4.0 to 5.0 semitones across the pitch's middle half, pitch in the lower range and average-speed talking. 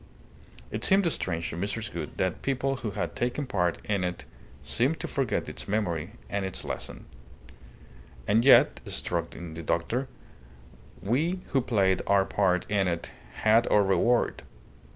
No: wide, 5.4 semitones; low, 100 Hz; average, 150 wpm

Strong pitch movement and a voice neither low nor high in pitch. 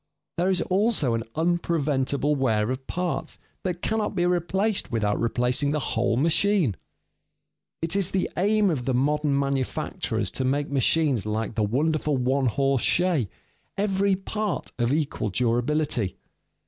Yes: wide, 6.0 semitones; medium, 145 Hz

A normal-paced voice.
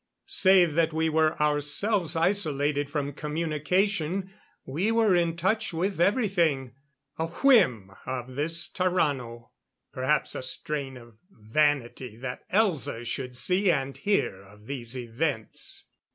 No: slow, 125 wpm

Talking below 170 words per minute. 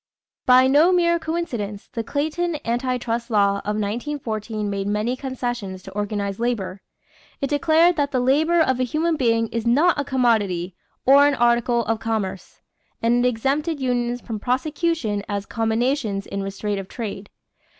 Yes: average, 160 wpm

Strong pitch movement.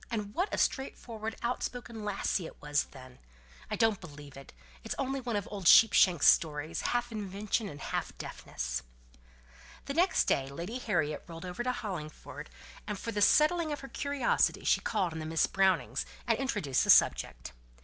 Yes: wide, 7.2 semitones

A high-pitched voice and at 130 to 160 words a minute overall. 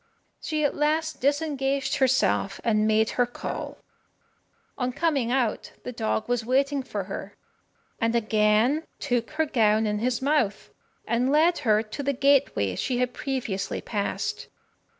Yes: very high, 250 Hz; average, 145 wpm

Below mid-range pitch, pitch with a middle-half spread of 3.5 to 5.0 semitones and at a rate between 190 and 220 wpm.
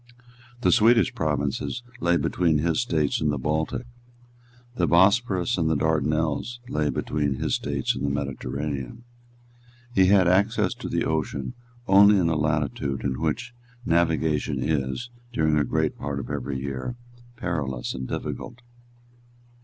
No: very low, 80 Hz; average, 4.7 semitones; average, 140 wpm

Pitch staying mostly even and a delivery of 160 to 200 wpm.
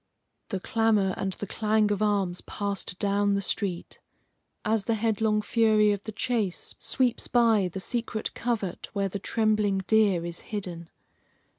No: narrow, 2.2 semitones; average, 150 wpm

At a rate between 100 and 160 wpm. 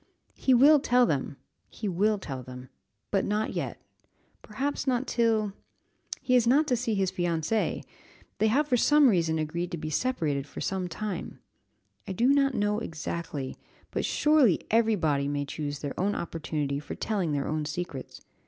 No: average, 170 wpm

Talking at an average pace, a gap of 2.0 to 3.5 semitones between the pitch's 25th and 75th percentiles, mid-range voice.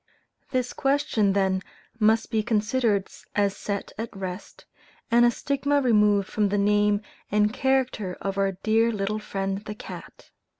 No: average, 145 wpm; average, 2.8 semitones; high, 210 Hz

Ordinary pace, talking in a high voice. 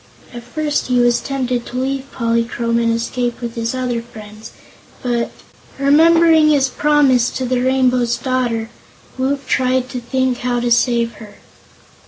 Yes: average, 150 wpm; very high, 250 Hz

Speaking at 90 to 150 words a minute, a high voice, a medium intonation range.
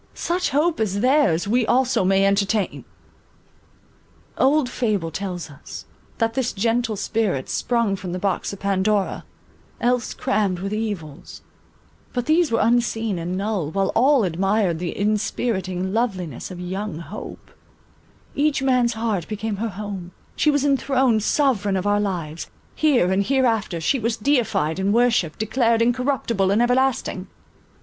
Yes: average, 145 wpm; high, 215 Hz; average, 4.4 semitones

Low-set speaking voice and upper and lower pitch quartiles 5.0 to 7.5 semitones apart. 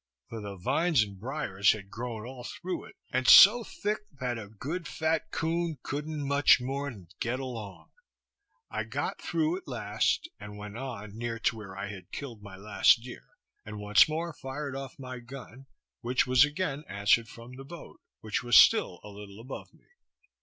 Yes: low, 125 Hz; wide, 5.4 semitones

